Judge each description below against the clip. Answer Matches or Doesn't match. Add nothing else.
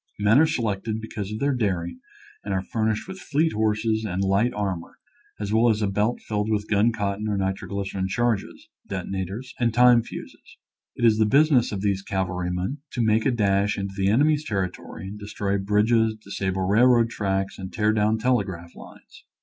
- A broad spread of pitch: Doesn't match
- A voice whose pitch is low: Matches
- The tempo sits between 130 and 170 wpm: Doesn't match